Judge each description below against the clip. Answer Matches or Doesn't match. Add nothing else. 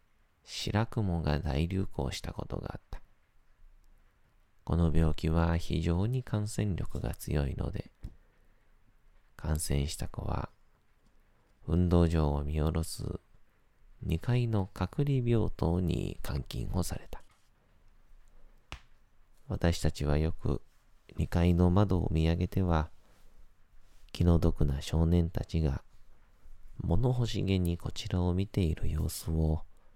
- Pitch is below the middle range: Matches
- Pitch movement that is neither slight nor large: Matches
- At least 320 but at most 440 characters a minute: Doesn't match